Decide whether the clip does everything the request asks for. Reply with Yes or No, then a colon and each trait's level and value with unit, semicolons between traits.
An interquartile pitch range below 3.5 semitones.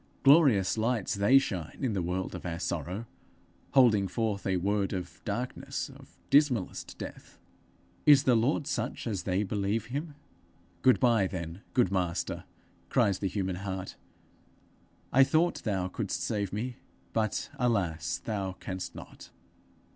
No: average, 4.8 semitones